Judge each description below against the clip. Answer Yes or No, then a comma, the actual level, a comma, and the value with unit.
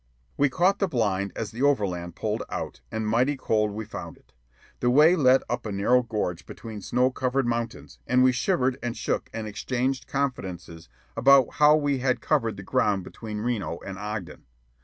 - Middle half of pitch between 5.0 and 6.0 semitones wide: No, average, 3.9 semitones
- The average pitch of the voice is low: Yes, low, 120 Hz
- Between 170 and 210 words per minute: Yes, average, 180 wpm